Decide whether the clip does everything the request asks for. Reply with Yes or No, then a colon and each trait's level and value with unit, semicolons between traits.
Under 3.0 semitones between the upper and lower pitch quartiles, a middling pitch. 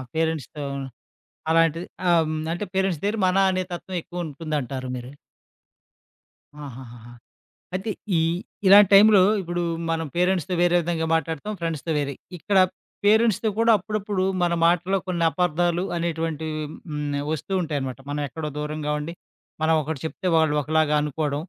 No: average, 3.3 semitones; medium, 165 Hz